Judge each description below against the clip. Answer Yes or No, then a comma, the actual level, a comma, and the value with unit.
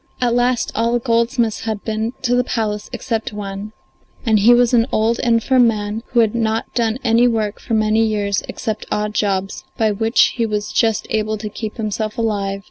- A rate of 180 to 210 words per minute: Yes, average, 195 wpm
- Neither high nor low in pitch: No, high, 220 Hz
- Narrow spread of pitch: Yes, narrow, 1.7 semitones